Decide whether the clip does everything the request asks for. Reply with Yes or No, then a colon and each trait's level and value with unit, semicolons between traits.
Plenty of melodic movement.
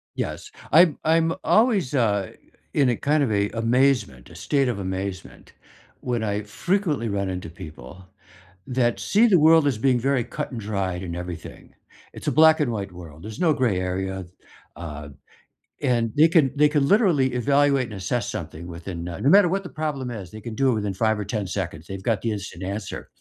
Yes: wide, 7.0 semitones